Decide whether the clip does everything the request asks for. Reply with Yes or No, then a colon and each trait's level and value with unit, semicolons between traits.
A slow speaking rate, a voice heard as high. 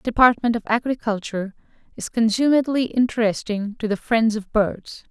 Yes: slow, 130 wpm; high, 225 Hz